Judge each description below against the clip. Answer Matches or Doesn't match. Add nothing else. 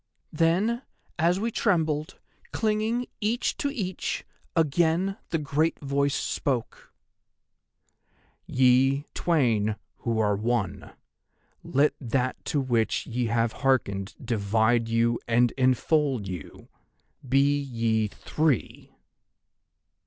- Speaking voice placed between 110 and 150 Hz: Matches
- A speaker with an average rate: Doesn't match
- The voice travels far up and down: Matches